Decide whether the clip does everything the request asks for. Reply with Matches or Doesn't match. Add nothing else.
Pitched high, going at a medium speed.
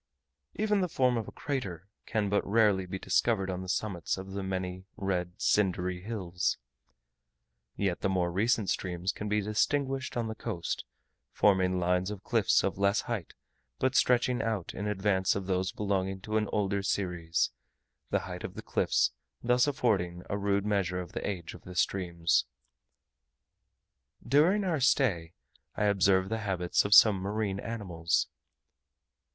Doesn't match